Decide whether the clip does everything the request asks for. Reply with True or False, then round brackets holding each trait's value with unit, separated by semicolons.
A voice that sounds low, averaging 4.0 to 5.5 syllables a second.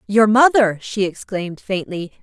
False (205 Hz; 4.6 syllables/s)